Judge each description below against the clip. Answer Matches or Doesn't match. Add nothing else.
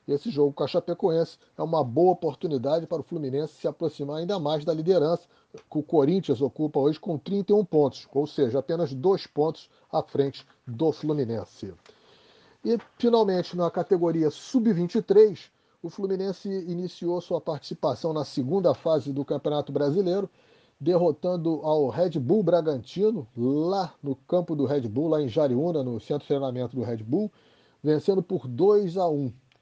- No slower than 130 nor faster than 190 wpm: Matches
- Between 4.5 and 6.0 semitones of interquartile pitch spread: Doesn't match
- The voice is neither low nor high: Matches